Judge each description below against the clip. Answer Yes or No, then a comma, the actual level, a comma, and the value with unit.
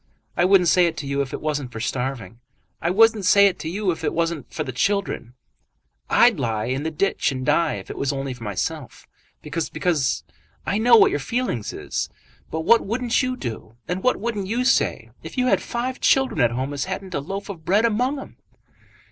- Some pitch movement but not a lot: No, wide, 7.4 semitones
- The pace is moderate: No, fast, 215 wpm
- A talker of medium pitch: Yes, medium, 170 Hz